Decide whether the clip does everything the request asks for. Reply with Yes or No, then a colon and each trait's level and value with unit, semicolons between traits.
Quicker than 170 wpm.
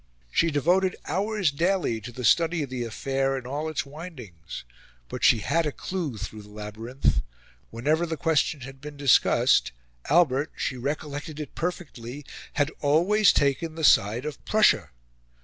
No: average, 155 wpm